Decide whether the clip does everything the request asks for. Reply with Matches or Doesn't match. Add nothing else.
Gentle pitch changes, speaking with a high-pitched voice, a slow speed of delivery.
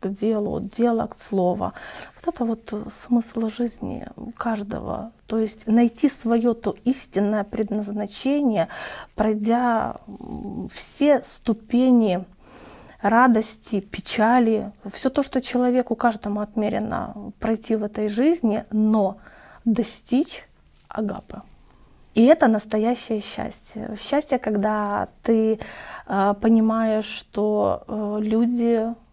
Matches